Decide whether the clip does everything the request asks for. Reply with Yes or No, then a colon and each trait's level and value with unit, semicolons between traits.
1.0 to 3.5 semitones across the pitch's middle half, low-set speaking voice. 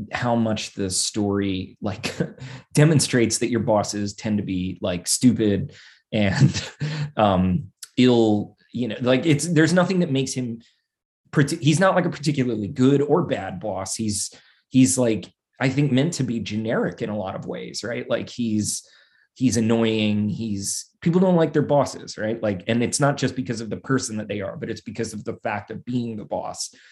No: average, 4.3 semitones; low, 115 Hz